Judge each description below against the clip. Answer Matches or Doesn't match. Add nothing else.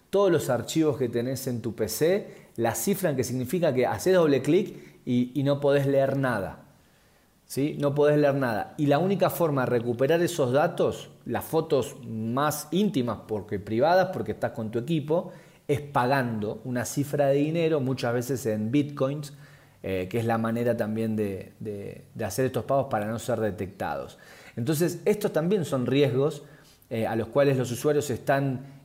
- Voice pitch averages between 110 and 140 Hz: Matches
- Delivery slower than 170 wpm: Doesn't match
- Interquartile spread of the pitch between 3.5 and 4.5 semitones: Matches